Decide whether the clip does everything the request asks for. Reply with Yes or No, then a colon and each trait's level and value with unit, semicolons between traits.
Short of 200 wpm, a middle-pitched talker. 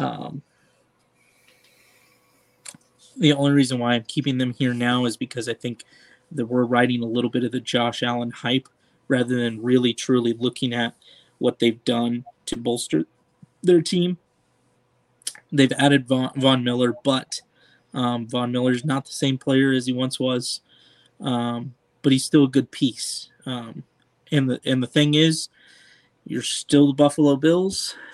No: average, 160 wpm; low, 125 Hz